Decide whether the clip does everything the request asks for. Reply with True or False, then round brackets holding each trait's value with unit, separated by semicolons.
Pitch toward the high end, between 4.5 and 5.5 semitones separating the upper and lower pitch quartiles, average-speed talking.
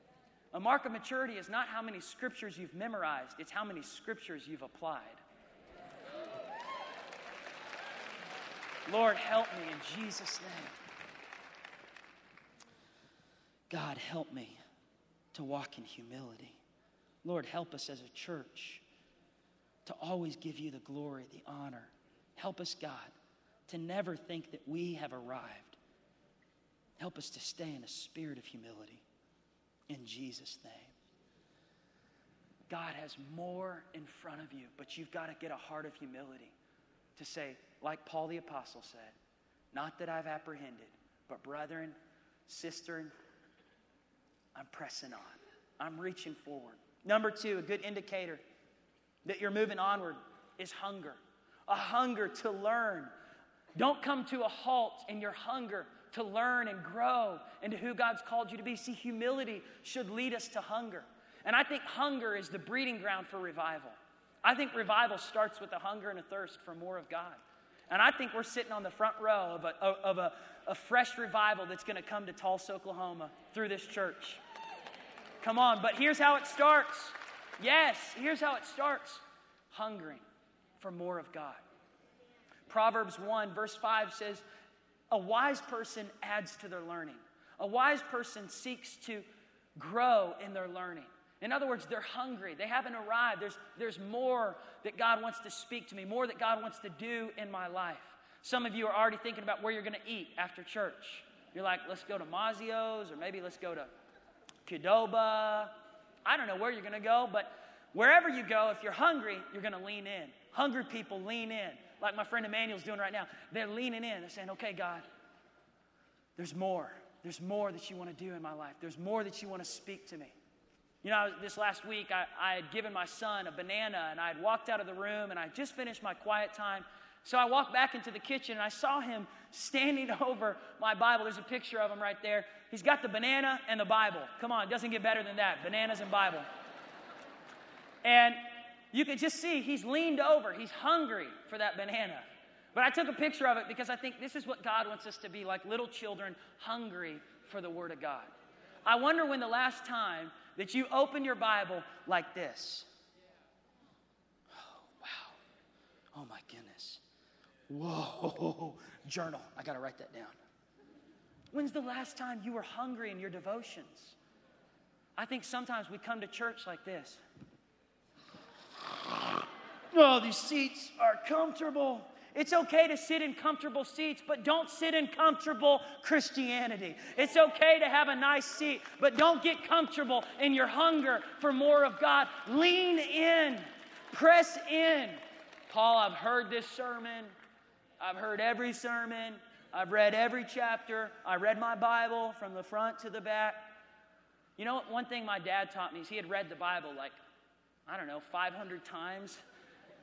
True (220 Hz; 5.2 semitones; 175 wpm)